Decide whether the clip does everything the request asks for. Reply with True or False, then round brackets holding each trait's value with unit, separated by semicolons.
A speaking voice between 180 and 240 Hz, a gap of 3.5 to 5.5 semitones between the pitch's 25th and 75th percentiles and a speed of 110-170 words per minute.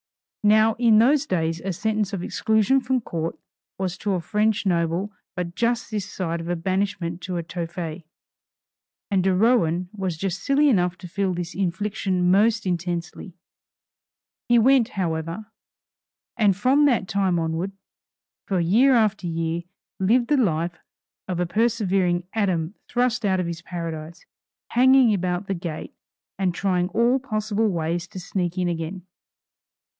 True (190 Hz; 4.0 semitones; 150 wpm)